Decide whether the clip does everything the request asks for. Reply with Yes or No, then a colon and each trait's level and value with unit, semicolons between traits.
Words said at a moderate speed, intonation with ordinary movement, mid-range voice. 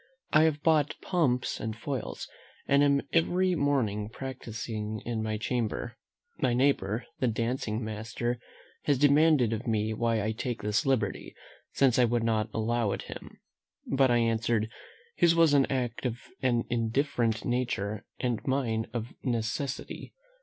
No: average, 145 wpm; average, 3.5 semitones; low, 120 Hz